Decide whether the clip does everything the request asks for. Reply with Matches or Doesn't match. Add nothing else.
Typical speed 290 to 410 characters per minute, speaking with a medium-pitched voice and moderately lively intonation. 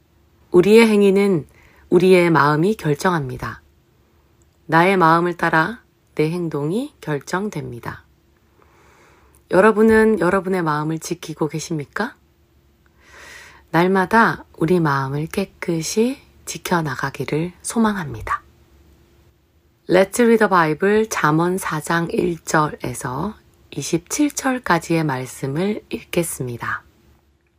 Doesn't match